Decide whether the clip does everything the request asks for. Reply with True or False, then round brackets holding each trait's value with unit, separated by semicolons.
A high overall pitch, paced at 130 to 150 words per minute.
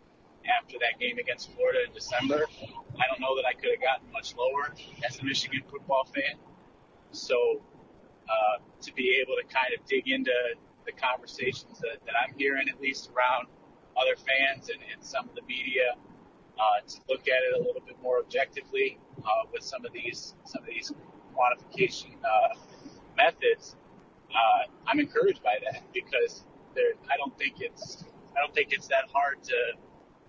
False (360 Hz; 170 wpm)